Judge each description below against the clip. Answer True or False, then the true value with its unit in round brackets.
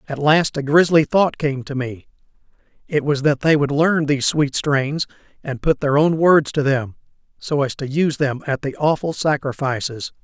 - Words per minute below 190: False (195 wpm)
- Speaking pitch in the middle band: True (145 Hz)